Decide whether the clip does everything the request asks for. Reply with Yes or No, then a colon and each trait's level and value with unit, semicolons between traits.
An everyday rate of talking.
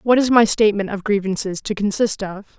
No: fast, 210 wpm